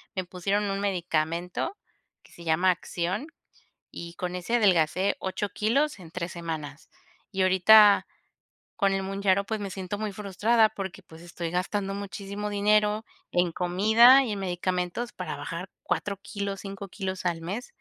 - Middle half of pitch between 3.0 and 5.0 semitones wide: No, narrow, 2.6 semitones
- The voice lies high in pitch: Yes, high, 195 Hz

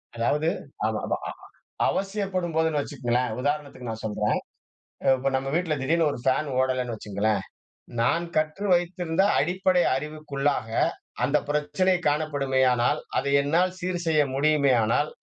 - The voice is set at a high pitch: No, medium, 145 Hz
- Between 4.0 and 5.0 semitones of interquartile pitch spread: Yes, average, 4.6 semitones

